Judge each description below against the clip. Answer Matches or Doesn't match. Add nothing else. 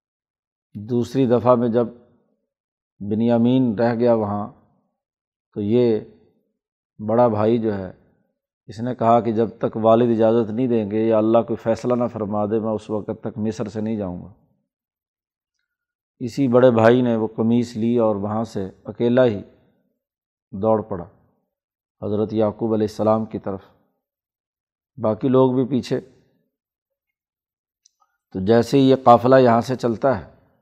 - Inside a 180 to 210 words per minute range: Doesn't match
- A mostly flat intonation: Matches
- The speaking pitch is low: Matches